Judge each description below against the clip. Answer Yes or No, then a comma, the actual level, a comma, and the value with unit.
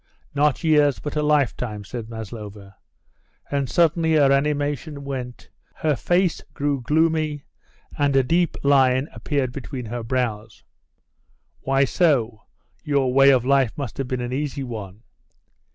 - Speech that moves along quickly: No, slow, 135 wpm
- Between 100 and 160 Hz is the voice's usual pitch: Yes, low, 135 Hz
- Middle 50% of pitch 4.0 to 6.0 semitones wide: No, average, 3.3 semitones